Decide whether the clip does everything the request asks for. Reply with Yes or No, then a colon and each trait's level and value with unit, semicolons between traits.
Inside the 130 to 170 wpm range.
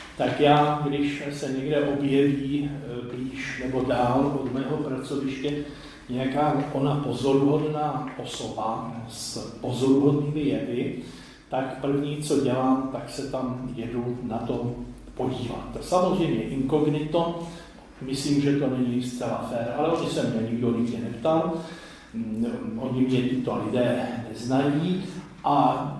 No: average, 120 wpm